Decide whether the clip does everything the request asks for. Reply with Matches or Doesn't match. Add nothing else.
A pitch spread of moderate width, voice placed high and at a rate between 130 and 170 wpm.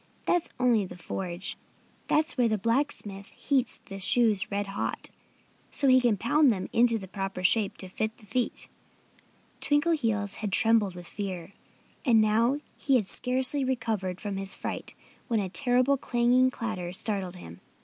Matches